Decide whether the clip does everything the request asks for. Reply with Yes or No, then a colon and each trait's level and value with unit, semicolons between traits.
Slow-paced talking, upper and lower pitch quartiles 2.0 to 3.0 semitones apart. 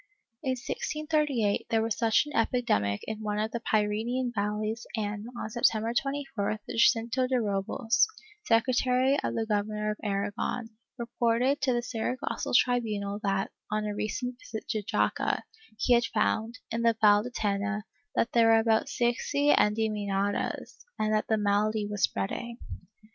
No: average, 155 wpm; narrow, 2.4 semitones